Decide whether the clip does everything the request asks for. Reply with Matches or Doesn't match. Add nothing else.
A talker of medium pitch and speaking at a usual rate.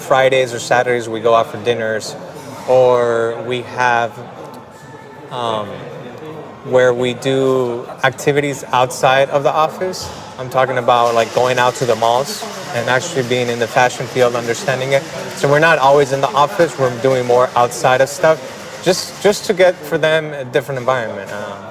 Doesn't match